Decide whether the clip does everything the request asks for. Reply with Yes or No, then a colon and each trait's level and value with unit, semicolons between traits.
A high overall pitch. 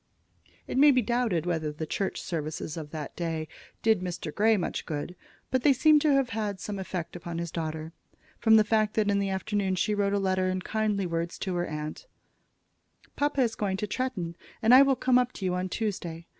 Yes: high, 195 Hz